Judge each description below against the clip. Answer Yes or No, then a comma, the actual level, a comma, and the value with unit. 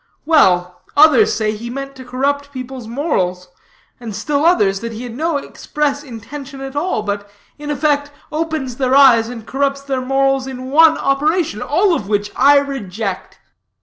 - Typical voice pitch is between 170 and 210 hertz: No, very high, 270 Hz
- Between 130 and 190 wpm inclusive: Yes, average, 165 wpm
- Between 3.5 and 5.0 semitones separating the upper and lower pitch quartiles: Yes, average, 4.2 semitones